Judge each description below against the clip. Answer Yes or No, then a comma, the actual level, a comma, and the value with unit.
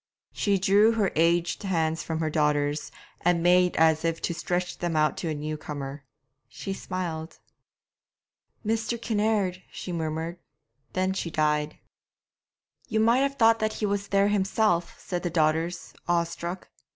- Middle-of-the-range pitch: Yes, medium, 175 Hz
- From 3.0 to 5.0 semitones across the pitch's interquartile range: Yes, average, 3.9 semitones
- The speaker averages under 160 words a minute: Yes, average, 150 wpm